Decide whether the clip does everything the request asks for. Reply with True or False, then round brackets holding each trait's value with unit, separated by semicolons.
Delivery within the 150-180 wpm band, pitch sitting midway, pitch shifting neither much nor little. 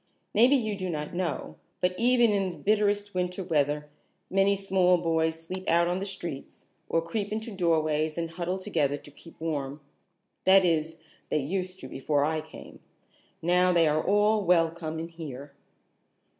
True (165 wpm; 170 Hz; 3.6 semitones)